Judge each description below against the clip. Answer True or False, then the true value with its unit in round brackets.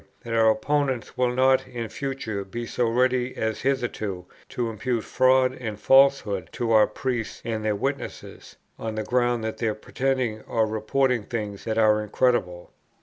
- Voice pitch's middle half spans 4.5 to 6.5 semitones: False (3.0 semitones)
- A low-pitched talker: True (115 Hz)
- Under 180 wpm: True (160 wpm)